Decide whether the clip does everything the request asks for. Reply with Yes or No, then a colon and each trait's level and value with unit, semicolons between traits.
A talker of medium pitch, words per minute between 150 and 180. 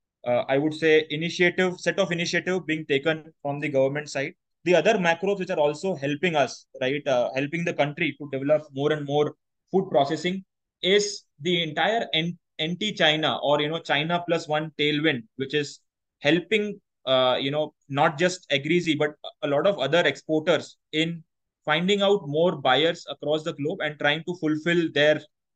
Yes: medium, 155 Hz; average, 170 wpm